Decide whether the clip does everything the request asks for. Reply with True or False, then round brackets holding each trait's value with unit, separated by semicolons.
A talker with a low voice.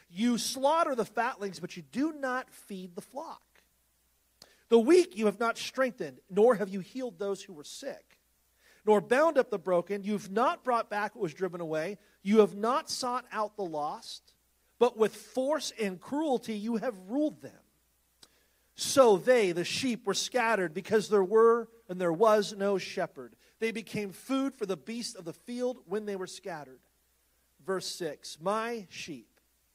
False (210 Hz)